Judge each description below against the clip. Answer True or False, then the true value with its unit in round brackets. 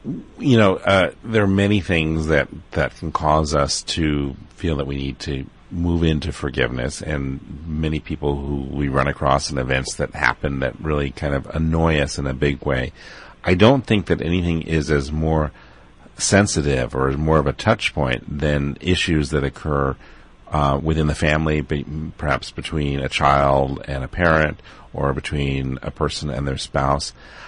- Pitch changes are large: False (2.4 semitones)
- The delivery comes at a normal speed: True (180 wpm)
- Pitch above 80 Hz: False (75 Hz)